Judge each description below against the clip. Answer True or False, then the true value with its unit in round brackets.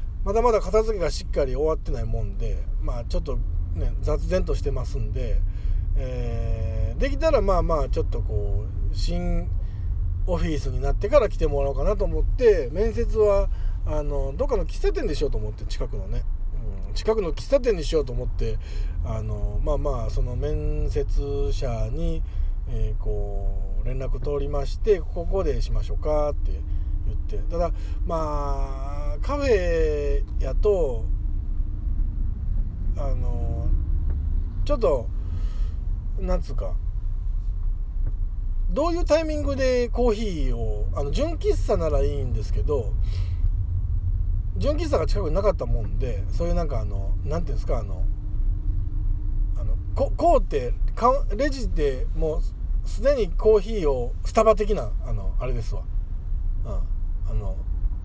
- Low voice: True (95 Hz)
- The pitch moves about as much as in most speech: True (4.9 semitones)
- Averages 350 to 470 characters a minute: False (285 characters per minute)